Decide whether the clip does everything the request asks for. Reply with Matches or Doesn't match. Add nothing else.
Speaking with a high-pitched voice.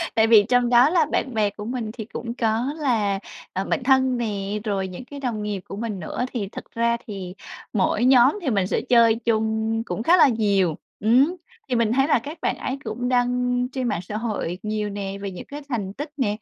Matches